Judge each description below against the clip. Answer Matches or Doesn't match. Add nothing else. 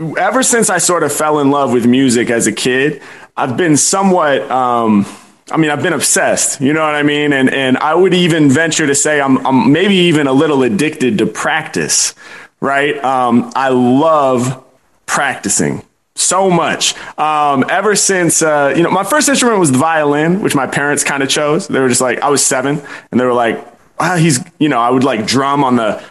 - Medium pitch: Matches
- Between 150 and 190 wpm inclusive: Doesn't match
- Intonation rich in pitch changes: Doesn't match